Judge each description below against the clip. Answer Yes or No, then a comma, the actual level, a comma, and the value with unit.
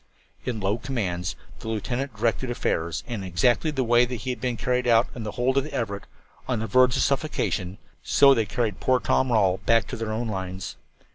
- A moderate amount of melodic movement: Yes, average, 3.8 semitones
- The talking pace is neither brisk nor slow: No, fast, 220 wpm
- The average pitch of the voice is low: Yes, low, 115 Hz